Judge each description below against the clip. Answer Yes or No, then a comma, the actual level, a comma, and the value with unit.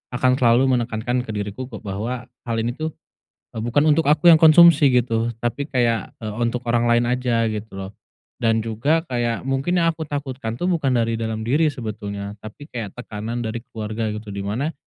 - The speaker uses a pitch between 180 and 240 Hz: No, low, 120 Hz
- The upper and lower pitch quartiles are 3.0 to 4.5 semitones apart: Yes, average, 3.3 semitones